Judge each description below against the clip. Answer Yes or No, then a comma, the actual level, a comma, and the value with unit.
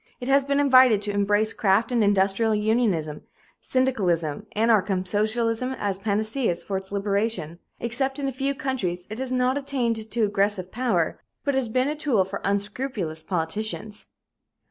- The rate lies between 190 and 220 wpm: No, average, 155 wpm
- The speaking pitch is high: Yes, high, 215 Hz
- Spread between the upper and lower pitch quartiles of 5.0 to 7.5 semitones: No, average, 4.5 semitones